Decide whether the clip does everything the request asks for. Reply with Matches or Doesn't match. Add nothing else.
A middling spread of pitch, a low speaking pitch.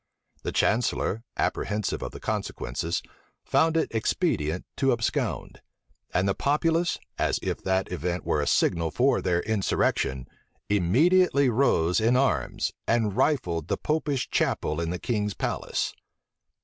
Doesn't match